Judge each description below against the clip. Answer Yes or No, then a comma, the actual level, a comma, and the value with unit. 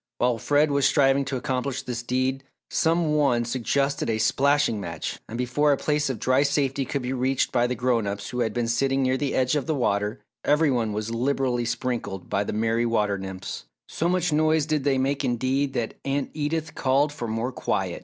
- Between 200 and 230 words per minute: Yes, fast, 205 wpm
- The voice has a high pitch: No, low, 130 Hz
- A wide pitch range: No, average, 3.3 semitones